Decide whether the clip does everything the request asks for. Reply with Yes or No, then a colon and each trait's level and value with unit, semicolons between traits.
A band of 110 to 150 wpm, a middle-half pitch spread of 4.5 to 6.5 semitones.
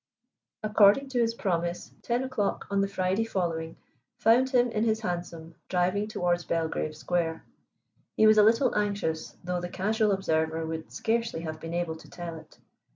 No: average, 165 wpm; average, 4.8 semitones